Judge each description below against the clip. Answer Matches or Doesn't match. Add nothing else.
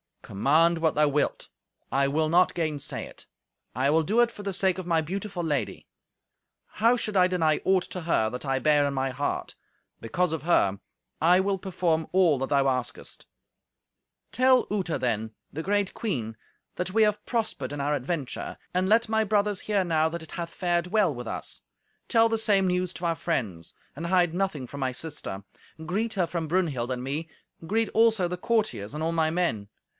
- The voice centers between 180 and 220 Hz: Doesn't match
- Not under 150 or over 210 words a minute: Matches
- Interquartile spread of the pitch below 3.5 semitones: Doesn't match